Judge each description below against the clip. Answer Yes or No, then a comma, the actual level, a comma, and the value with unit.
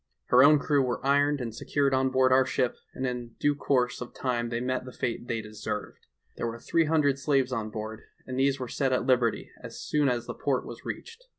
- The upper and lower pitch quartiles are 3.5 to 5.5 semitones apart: No, average, 2.7 semitones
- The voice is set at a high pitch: No, low, 130 Hz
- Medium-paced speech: No, fast, 225 wpm